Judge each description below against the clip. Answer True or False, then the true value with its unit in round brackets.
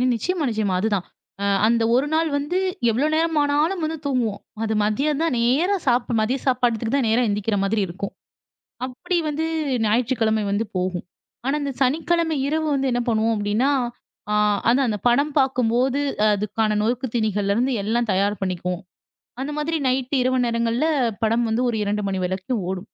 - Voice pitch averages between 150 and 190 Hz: False (240 Hz)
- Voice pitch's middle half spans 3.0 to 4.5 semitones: False (4.9 semitones)